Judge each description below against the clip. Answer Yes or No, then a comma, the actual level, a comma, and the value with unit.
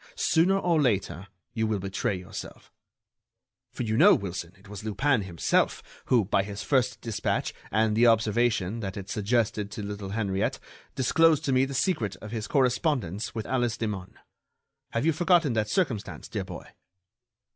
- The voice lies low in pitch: Yes, low, 110 Hz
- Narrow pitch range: No, average, 4.5 semitones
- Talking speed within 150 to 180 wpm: Yes, average, 160 wpm